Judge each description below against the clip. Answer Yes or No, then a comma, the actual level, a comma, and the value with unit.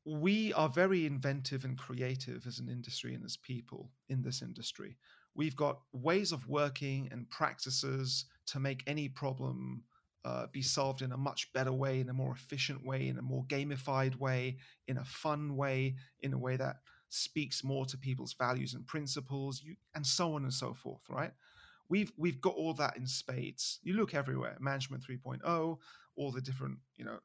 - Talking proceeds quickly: No, average, 185 wpm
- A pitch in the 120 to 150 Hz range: Yes, low, 135 Hz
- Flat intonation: Yes, narrow, 2.1 semitones